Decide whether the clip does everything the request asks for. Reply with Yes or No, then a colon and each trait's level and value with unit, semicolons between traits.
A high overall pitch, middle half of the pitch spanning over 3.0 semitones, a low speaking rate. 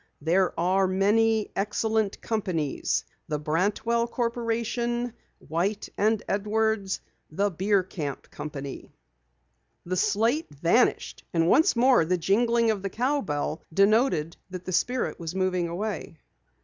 Yes: high, 200 Hz; average, 4.6 semitones; slow, 115 wpm